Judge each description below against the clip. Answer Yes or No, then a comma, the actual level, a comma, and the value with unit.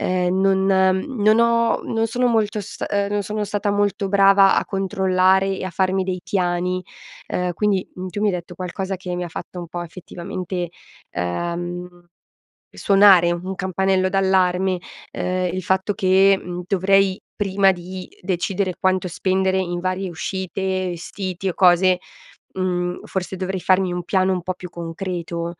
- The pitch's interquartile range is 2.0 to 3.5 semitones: No, narrow, 1.5 semitones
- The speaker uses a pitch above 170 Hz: Yes, medium, 185 Hz